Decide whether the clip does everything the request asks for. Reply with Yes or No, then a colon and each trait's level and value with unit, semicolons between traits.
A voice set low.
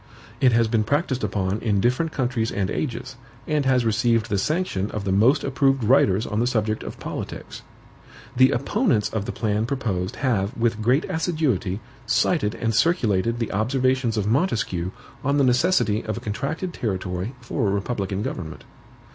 Yes: low, 115 Hz